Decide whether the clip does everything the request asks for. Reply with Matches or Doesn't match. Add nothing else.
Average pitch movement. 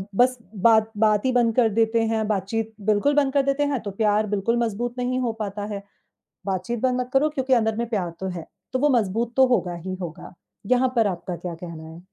Matches